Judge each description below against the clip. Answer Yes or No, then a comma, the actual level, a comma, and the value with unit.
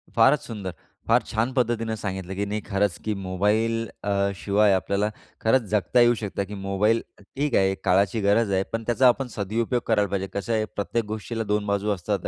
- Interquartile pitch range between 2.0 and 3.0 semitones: Yes, narrow, 2.4 semitones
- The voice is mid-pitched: No, low, 105 Hz